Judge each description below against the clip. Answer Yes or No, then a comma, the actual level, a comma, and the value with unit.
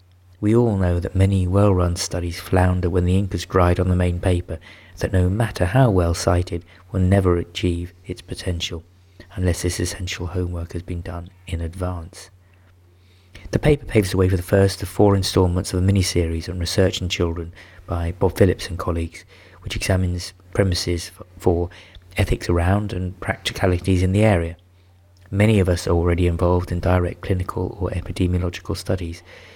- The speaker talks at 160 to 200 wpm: Yes, average, 170 wpm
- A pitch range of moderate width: No, narrow, 1.6 semitones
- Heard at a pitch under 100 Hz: Yes, very low, 90 Hz